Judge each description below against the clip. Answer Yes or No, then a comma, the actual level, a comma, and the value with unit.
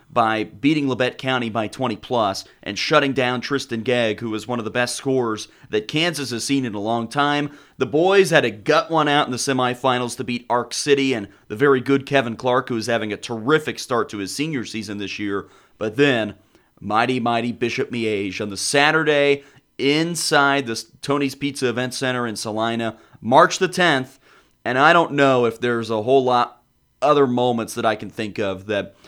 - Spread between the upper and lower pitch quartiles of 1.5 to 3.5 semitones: No, average, 3.9 semitones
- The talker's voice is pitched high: No, low, 125 Hz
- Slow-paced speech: No, average, 200 wpm